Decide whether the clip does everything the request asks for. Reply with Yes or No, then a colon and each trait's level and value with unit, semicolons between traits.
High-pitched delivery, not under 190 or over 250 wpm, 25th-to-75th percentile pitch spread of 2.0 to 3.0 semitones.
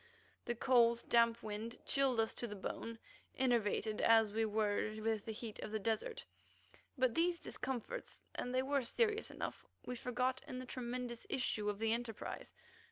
No: high, 235 Hz; average, 165 wpm; narrow, 2.6 semitones